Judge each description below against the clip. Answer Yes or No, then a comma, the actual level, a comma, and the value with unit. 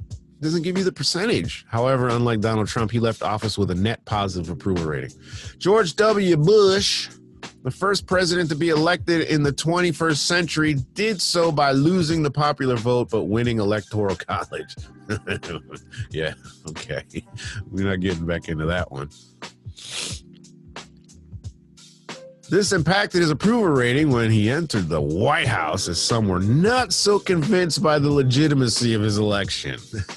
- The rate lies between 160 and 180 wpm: No, average, 145 wpm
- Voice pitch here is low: Yes, low, 130 Hz